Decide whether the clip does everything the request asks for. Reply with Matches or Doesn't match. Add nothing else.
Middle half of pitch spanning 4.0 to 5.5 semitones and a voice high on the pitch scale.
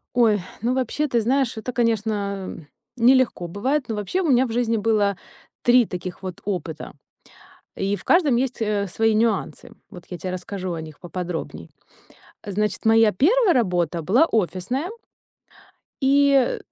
Matches